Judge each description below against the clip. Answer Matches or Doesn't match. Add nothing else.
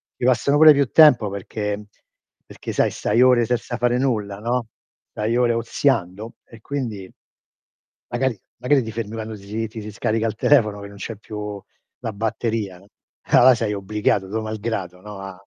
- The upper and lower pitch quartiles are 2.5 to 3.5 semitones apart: Matches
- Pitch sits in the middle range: Doesn't match